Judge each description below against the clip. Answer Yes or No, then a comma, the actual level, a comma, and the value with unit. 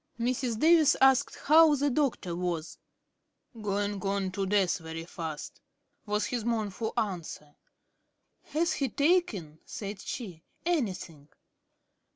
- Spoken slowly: Yes, slow, 115 wpm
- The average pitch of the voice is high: Yes, high, 205 Hz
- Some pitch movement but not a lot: No, wide, 6.9 semitones